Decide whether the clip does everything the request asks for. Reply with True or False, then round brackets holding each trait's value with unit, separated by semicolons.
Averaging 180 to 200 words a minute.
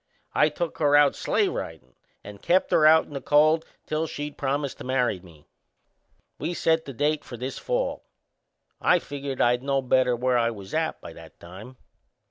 True (185 wpm)